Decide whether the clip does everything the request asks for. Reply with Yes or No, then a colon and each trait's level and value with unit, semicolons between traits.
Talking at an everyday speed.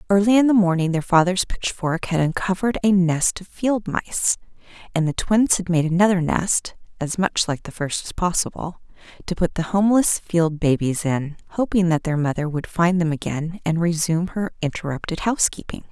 Yes: average, 180 wpm